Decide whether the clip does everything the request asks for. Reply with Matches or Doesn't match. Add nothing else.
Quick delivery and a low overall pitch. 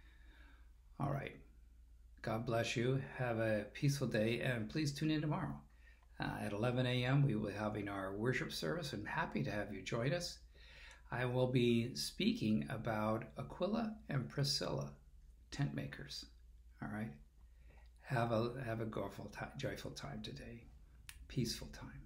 Doesn't match